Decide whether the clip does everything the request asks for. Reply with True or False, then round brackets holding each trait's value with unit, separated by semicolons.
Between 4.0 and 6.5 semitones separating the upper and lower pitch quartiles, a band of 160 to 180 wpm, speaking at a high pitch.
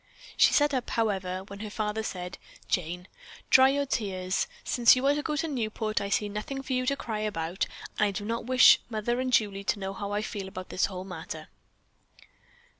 False (4.7 semitones; 205 wpm; 210 Hz)